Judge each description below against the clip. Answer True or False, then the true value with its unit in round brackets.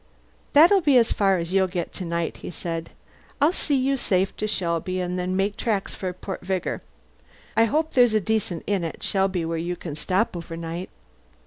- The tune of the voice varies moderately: True (4.2 semitones)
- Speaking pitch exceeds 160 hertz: True (190 Hz)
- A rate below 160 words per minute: False (195 wpm)